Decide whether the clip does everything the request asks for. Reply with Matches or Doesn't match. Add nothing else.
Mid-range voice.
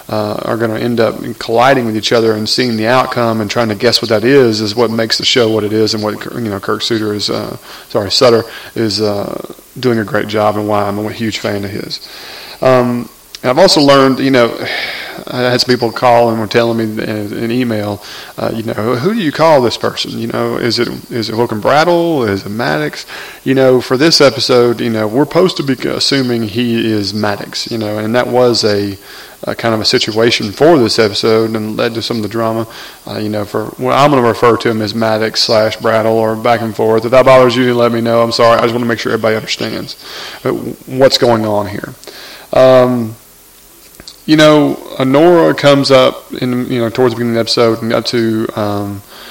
Doesn't match